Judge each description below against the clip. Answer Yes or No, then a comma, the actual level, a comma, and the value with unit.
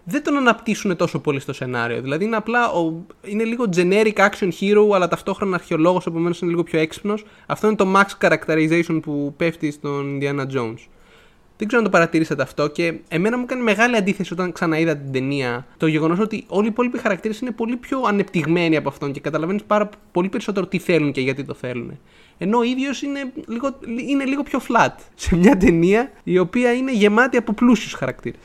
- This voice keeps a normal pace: No, fast, 195 wpm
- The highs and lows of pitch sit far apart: Yes, wide, 6.1 semitones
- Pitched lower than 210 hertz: Yes, medium, 185 Hz